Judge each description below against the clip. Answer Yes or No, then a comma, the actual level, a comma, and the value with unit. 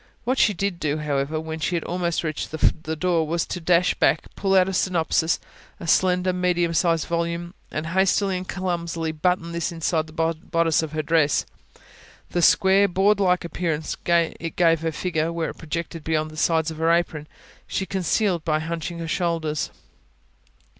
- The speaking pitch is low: No, medium, 170 Hz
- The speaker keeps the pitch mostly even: Yes, narrow, 2.1 semitones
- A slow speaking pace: No, average, 180 wpm